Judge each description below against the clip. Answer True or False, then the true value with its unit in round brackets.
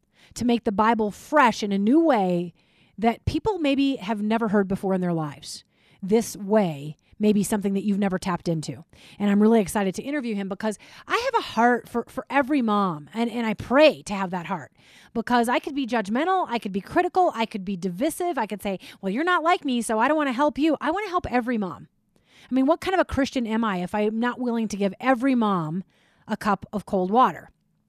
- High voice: True (225 Hz)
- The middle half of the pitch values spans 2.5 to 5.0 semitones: False (5.5 semitones)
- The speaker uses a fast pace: True (230 wpm)